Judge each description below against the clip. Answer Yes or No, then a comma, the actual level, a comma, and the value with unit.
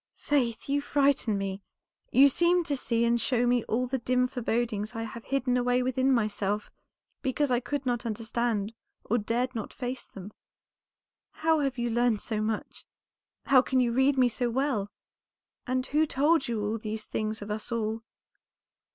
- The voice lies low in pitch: No, high, 245 Hz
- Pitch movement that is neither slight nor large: Yes, average, 3.0 semitones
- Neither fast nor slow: Yes, average, 170 wpm